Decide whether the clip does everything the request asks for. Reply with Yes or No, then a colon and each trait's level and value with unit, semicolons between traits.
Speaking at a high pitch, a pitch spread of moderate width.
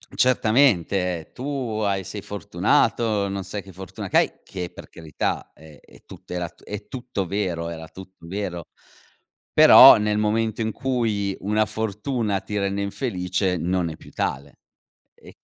No: low, 100 Hz; average, 3.1 semitones